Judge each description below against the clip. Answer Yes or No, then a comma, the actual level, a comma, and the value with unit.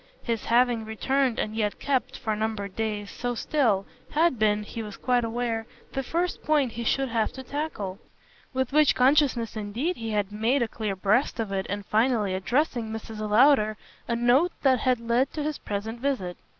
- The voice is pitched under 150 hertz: No, high, 230 Hz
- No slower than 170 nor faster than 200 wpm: Yes, average, 185 wpm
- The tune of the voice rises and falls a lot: No, average, 3.7 semitones